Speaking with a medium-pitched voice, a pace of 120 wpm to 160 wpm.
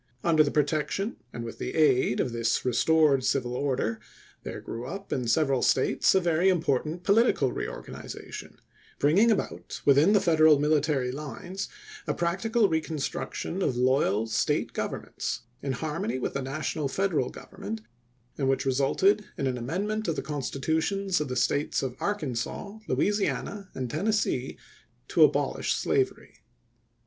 Yes: medium, 150 Hz; average, 145 wpm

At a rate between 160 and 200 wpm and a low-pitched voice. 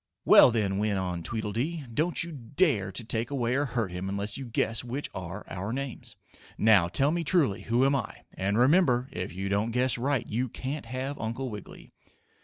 Yes: average, 195 wpm; low, 115 Hz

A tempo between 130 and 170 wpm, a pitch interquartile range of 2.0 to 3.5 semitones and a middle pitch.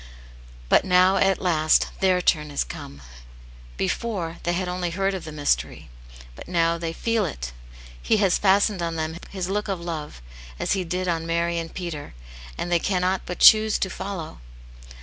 No: average, 180 wpm; average, 2.7 semitones; medium, 175 Hz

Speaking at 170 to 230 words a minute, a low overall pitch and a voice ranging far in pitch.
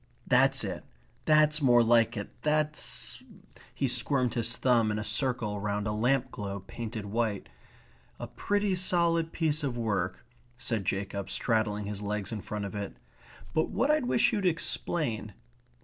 No: average, 160 wpm; low, 120 Hz; wide, 6.4 semitones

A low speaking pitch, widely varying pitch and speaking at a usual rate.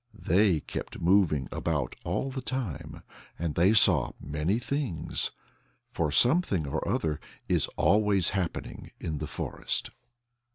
No: very low, 85 Hz; wide, 5.8 semitones; slow, 125 wpm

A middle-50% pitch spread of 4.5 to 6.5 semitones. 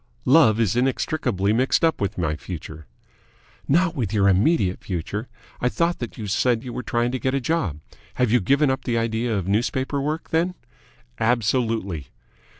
Yes: average, 5.1 semitones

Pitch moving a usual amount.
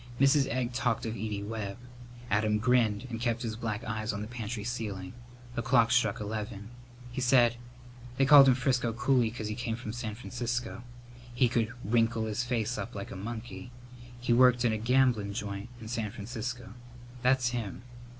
No: narrow, 2.3 semitones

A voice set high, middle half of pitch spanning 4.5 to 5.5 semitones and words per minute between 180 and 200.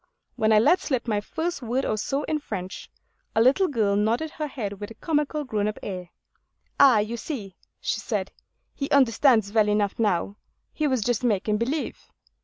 Yes: high, 225 Hz; average, 5.1 semitones; average, 185 wpm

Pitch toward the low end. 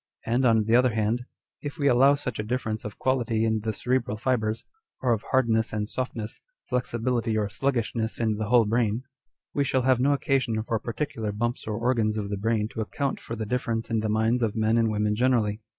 Yes: low, 115 Hz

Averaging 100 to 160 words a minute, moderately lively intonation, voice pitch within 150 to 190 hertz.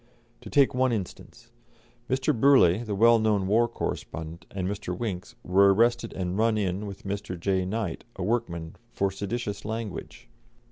No: average, 155 wpm; average, 3.7 semitones; low, 100 Hz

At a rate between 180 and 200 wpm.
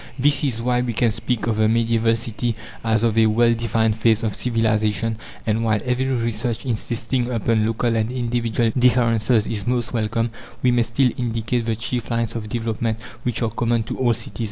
Yes: average, 190 wpm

